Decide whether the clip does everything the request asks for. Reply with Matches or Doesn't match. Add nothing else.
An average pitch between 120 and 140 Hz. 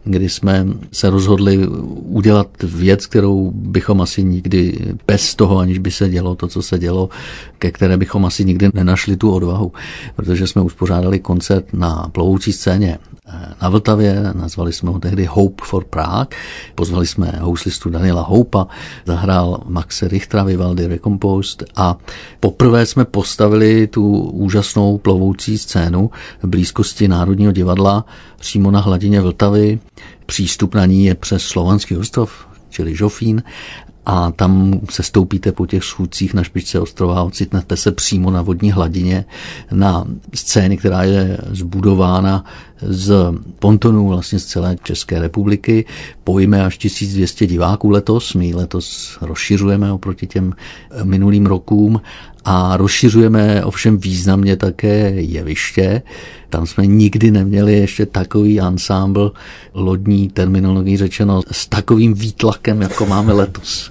Doesn't match